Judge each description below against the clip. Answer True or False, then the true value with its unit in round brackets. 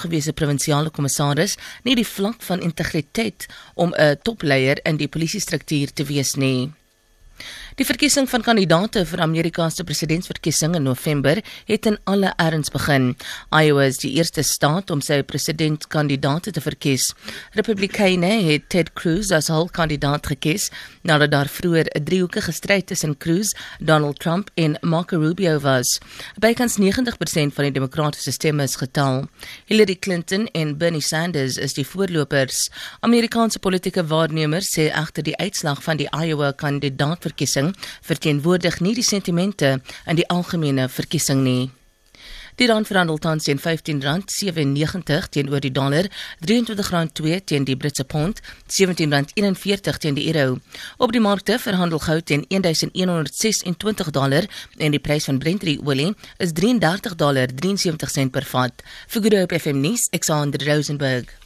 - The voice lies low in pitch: False (160 Hz)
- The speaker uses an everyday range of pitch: True (4.3 semitones)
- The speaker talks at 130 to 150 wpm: True (140 wpm)